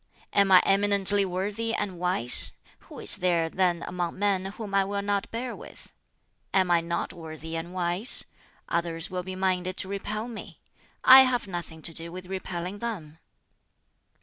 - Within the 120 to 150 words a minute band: No, average, 165 wpm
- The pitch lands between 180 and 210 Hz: Yes, medium, 185 Hz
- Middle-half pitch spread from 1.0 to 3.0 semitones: Yes, average, 2.7 semitones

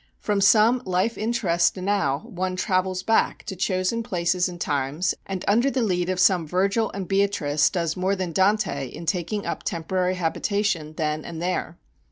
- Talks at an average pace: Yes, average, 170 wpm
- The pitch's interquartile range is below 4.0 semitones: Yes, average, 2.9 semitones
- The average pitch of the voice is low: No, medium, 185 Hz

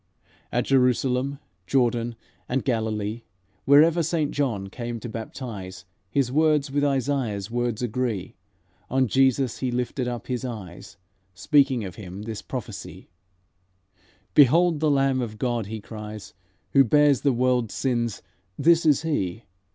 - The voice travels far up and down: No, average, 3.8 semitones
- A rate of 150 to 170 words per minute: No, slow, 135 wpm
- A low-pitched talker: Yes, low, 125 Hz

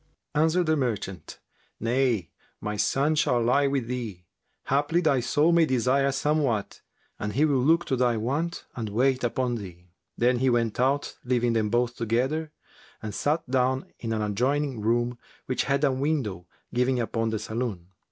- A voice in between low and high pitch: No, low, 125 Hz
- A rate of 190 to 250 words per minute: No, average, 165 wpm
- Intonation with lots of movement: No, average, 3.6 semitones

